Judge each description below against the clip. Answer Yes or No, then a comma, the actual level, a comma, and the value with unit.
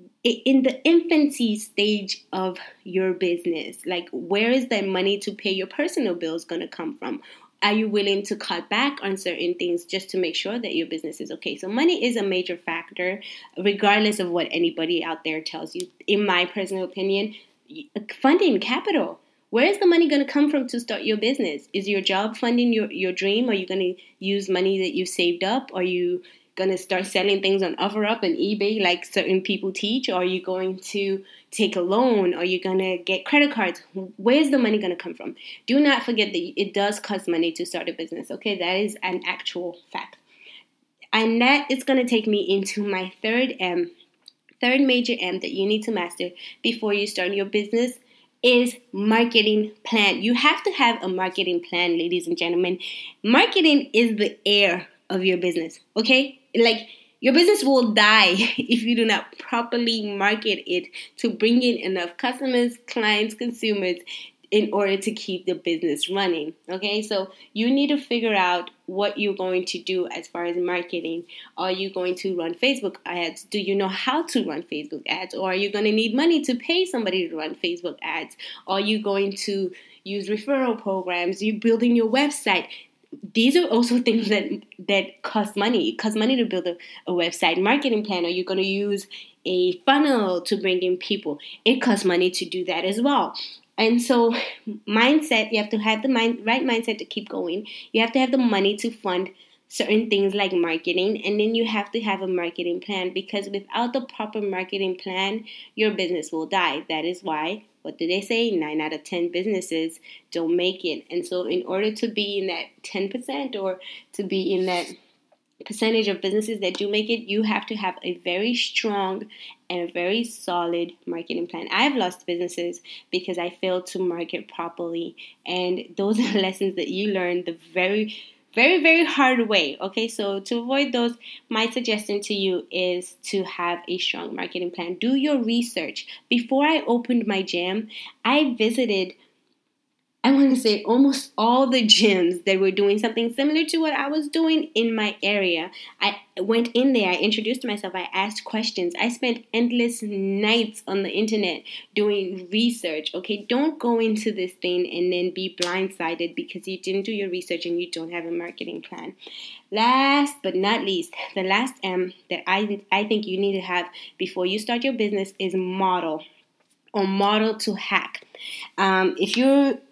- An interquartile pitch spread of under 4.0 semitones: No, average, 4.4 semitones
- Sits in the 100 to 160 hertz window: No, high, 205 Hz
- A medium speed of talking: Yes, average, 190 wpm